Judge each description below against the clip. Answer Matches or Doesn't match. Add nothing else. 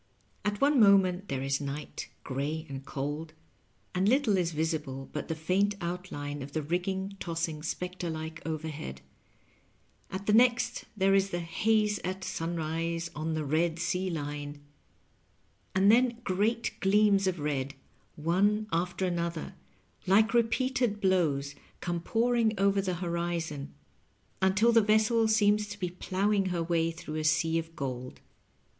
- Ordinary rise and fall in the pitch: Matches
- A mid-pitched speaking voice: Matches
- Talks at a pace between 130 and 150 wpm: Matches